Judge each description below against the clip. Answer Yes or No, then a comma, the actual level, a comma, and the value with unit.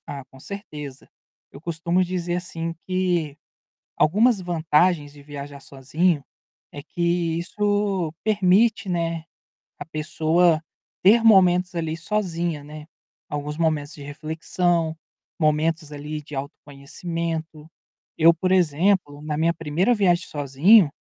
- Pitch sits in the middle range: Yes, medium, 165 Hz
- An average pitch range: Yes, average, 3.3 semitones